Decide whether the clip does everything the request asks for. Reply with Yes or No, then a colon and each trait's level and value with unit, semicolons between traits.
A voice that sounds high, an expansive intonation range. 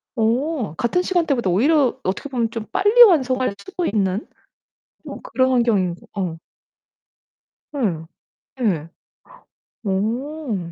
Yes: high, 235 Hz; wide, 7.0 semitones